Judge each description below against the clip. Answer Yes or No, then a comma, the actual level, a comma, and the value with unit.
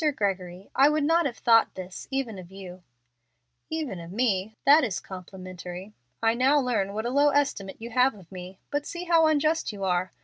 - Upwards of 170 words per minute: Yes, average, 200 wpm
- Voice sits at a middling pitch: No, high, 220 Hz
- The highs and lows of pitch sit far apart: Yes, wide, 7.2 semitones